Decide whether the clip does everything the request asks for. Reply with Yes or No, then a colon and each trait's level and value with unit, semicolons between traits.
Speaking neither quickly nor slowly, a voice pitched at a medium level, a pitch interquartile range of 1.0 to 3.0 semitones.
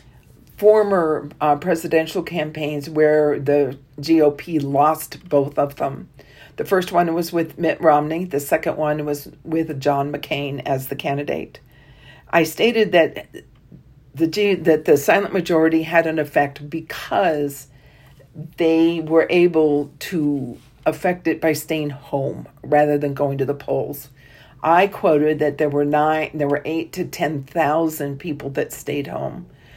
Yes: average, 145 wpm; medium, 150 Hz; narrow, 2.4 semitones